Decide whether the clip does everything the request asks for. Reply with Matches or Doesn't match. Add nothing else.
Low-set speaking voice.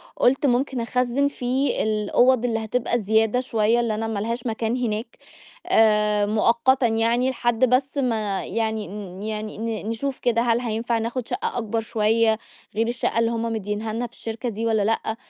Doesn't match